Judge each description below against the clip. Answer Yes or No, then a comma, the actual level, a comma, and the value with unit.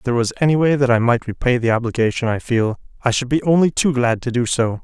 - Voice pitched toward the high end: No, low, 125 Hz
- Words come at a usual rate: No, fast, 275 wpm